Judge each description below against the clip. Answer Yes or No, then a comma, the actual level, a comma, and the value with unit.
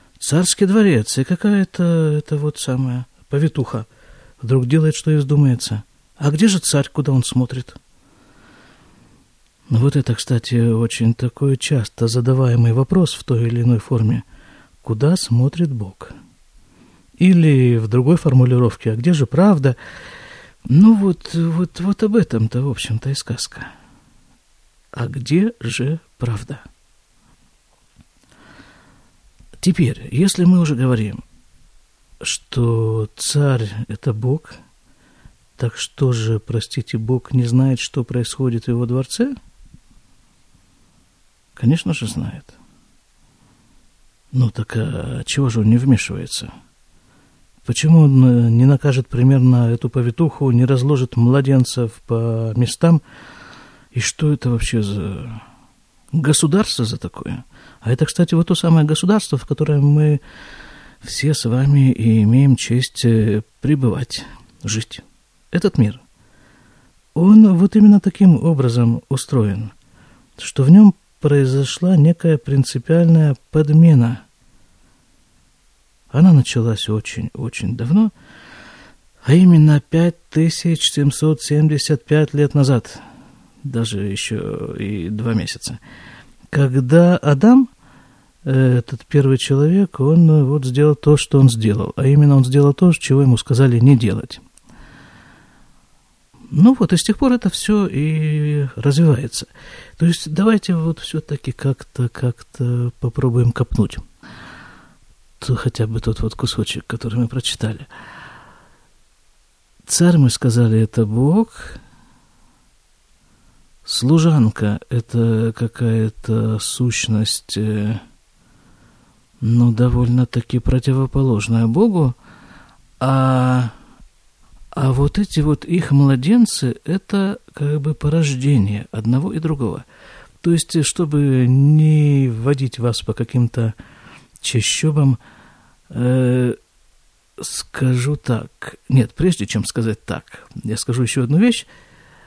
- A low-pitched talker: Yes, low, 130 Hz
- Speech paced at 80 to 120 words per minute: Yes, slow, 110 wpm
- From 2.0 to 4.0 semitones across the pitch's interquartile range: No, average, 4.6 semitones